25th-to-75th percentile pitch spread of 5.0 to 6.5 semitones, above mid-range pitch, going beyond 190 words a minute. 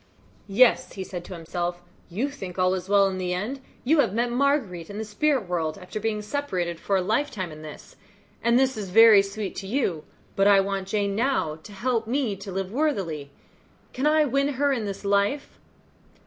Yes: wide, 5.5 semitones; high, 200 Hz; average, 200 wpm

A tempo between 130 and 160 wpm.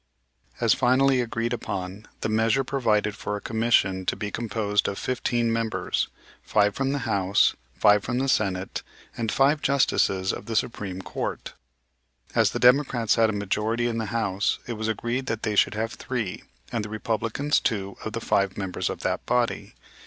No: average, 175 wpm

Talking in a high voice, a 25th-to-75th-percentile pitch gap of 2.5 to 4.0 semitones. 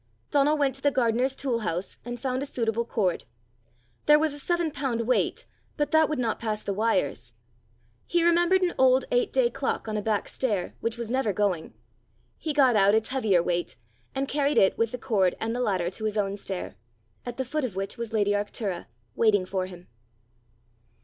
No: high, 230 Hz; average, 5.2 semitones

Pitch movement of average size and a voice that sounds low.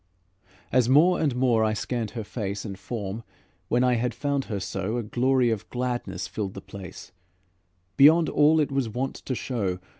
Yes: average, 3.8 semitones; low, 120 Hz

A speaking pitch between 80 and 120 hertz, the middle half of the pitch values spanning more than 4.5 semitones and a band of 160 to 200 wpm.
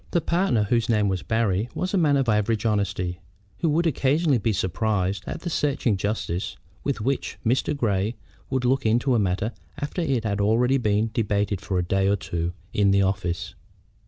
Yes: low, 110 Hz; average, 5.0 semitones; average, 190 wpm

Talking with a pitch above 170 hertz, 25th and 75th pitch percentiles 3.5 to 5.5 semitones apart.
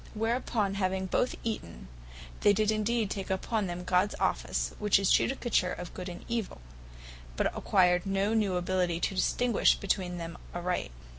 No: high, 190 Hz; average, 3.1 semitones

